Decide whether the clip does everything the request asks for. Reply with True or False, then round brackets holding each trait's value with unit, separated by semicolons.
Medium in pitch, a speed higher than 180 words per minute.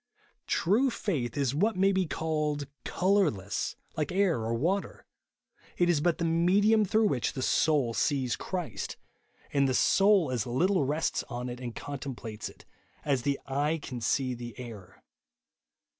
False (145 Hz; 155 wpm)